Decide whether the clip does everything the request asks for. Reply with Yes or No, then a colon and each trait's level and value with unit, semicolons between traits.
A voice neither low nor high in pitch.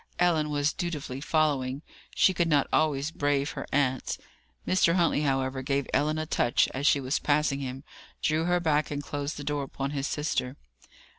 Yes: medium, 145 Hz